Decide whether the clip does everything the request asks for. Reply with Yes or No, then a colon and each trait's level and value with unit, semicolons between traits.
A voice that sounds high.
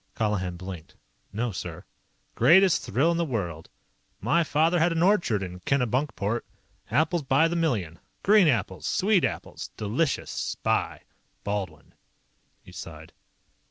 No: low, 125 Hz